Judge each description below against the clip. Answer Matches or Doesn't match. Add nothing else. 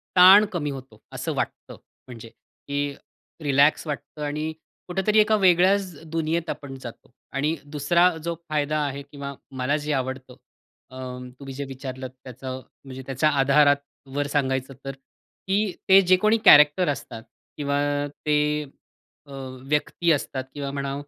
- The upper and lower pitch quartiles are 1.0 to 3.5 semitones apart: Matches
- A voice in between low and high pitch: Matches